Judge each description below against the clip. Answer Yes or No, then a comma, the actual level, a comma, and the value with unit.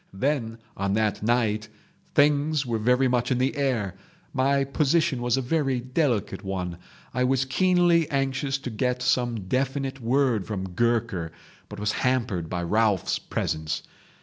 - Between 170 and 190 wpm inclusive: No, average, 150 wpm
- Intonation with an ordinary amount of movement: Yes, average, 4.2 semitones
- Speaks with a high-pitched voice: No, low, 125 Hz